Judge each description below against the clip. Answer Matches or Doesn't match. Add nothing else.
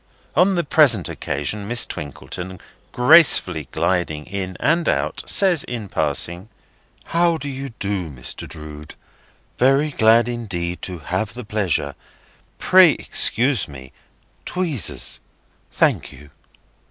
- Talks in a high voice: Doesn't match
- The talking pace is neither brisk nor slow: Doesn't match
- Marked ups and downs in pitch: Matches